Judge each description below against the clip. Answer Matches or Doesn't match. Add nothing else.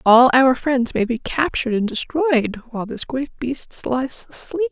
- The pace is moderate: Matches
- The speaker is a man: Doesn't match